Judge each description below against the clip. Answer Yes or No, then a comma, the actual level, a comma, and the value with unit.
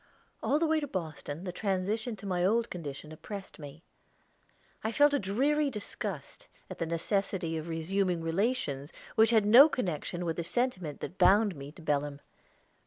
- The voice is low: No, high, 190 Hz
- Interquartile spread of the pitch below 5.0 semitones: No, wide, 5.4 semitones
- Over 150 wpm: Yes, average, 170 wpm